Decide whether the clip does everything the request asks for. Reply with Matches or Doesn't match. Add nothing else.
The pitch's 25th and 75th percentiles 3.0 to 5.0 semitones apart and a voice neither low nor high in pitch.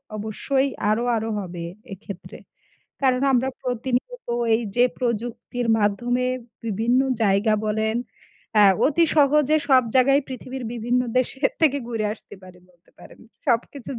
Doesn't match